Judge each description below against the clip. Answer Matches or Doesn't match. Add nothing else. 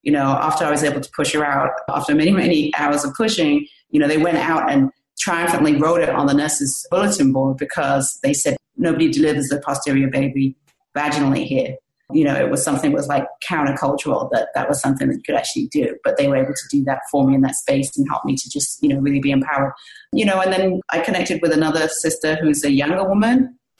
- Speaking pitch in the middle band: Matches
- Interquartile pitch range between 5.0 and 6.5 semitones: Matches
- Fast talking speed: Matches